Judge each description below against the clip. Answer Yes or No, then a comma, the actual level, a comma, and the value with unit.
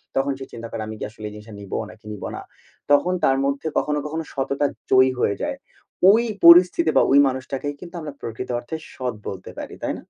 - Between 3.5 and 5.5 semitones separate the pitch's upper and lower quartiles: Yes, average, 4.8 semitones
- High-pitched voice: No, low, 135 Hz